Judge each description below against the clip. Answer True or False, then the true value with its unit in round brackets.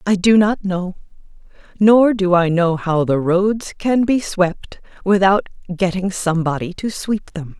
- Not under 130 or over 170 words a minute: True (160 wpm)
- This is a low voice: False (190 Hz)